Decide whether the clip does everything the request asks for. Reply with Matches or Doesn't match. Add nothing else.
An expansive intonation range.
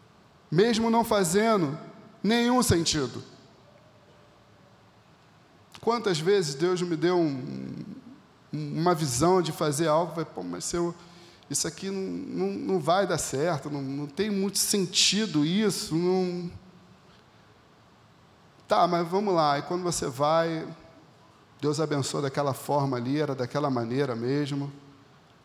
Doesn't match